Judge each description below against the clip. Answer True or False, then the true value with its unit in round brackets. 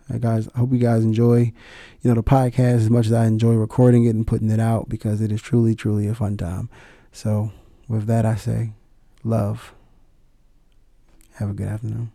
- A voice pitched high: False (115 Hz)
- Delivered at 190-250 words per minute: True (200 wpm)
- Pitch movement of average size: False (1.4 semitones)